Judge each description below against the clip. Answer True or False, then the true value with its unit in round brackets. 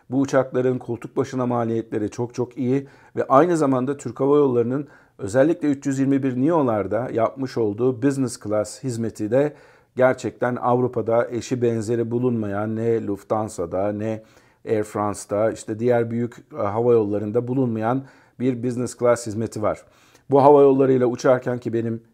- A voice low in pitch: True (120 Hz)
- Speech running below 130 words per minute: False (135 wpm)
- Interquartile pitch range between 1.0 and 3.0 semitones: True (2.7 semitones)